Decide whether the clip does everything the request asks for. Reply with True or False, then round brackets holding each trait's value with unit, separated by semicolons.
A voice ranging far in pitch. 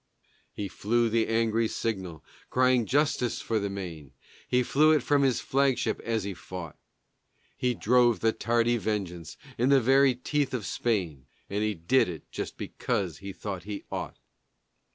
False (4.5 semitones)